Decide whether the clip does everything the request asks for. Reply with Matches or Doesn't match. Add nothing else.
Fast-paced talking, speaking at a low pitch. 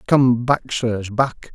Doesn't match